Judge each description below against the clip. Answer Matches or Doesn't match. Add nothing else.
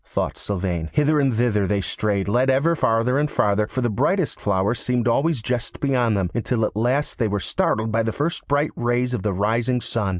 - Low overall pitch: Matches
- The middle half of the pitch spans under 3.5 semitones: Doesn't match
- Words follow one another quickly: Matches